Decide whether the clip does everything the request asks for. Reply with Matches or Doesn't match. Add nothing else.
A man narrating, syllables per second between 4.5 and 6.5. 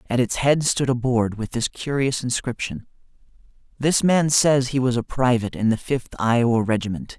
Matches